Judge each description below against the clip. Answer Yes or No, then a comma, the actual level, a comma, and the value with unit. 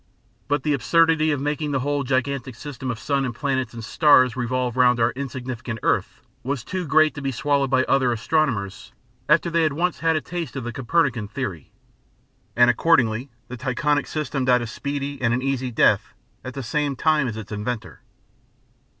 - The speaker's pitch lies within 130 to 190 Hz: Yes, low, 135 Hz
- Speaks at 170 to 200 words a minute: Yes, average, 185 wpm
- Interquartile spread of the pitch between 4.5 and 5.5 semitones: No, average, 3.2 semitones